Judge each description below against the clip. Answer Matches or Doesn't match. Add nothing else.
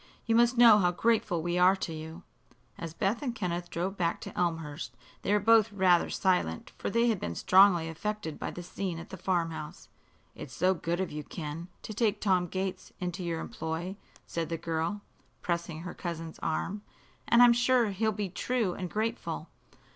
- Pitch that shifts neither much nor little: Matches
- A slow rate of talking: Doesn't match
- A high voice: Doesn't match